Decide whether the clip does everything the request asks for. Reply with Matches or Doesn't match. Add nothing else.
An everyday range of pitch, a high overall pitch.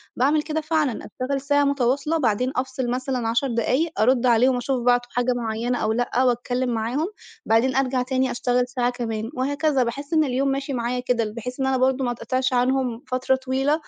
Doesn't match